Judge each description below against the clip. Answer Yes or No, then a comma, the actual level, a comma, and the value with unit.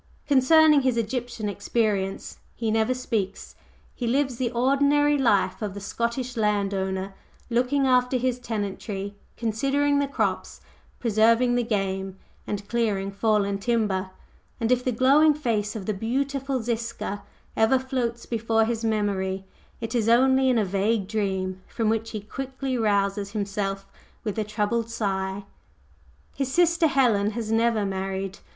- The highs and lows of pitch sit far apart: No, average, 3.9 semitones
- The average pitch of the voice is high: Yes, high, 225 Hz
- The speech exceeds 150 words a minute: No, average, 145 wpm